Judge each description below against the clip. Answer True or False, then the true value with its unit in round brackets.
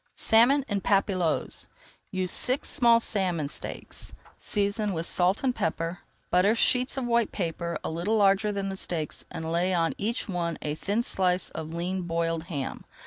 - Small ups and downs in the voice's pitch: False (4.0 semitones)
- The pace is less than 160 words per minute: False (165 wpm)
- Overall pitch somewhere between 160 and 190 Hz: True (185 Hz)